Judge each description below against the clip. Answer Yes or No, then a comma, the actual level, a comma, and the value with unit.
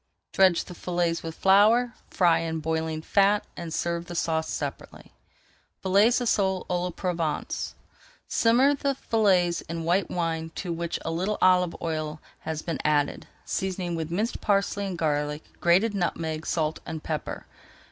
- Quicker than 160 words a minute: No, average, 155 wpm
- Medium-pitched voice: Yes, medium, 175 Hz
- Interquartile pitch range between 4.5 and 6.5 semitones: No, average, 3.1 semitones